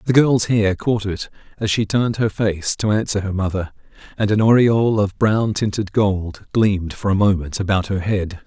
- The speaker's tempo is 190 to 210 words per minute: Yes, average, 200 wpm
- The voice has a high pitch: No, low, 100 Hz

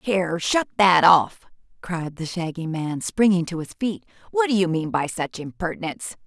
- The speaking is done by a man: No, female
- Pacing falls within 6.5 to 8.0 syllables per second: No, 4.9 syllables/s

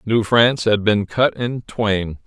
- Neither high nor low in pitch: No, low, 110 Hz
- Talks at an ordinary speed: Yes, average, 185 wpm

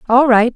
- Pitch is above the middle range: Yes, high, 245 Hz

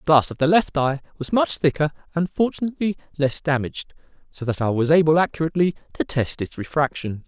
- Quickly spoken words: No, average, 190 wpm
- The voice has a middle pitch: Yes, medium, 150 Hz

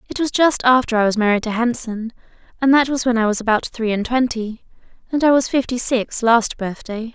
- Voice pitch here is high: Yes, high, 235 Hz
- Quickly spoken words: Yes, fast, 220 wpm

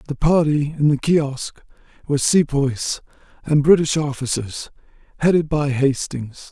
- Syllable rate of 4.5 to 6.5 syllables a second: No, 4.3 syllables/s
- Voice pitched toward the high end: No, medium, 145 Hz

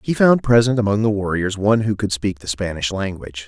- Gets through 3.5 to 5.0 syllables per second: No, 5.9 syllables/s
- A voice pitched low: Yes, low, 105 Hz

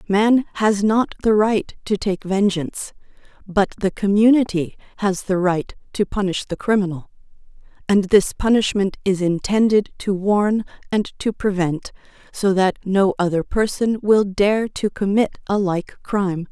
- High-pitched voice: Yes, high, 200 Hz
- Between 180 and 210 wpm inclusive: No, average, 145 wpm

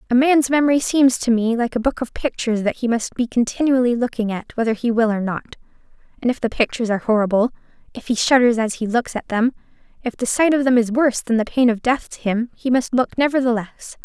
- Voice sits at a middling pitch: No, high, 240 Hz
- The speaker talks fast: Yes, fast, 235 wpm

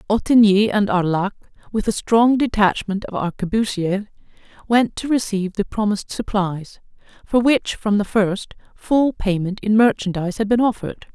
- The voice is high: Yes, high, 210 Hz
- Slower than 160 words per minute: Yes, average, 145 wpm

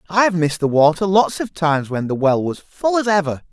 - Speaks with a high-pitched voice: No, medium, 170 Hz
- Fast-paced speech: Yes, fast, 240 wpm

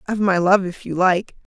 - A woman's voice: Yes, female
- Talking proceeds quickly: Yes, fast, 235 wpm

